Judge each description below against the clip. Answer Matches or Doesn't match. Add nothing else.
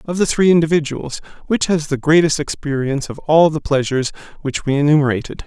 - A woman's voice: Doesn't match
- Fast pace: Doesn't match